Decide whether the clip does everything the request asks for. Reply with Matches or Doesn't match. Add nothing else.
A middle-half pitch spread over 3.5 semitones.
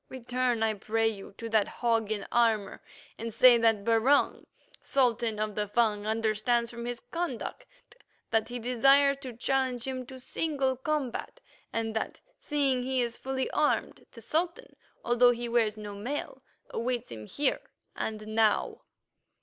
Doesn't match